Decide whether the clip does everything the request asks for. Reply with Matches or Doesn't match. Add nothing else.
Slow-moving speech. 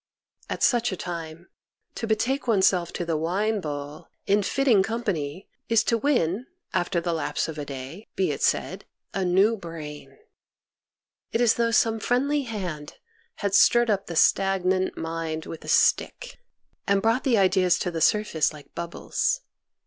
Doesn't match